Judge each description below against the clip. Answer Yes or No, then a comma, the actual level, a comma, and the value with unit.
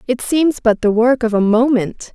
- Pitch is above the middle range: Yes, high, 235 Hz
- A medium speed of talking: No, fast, 225 wpm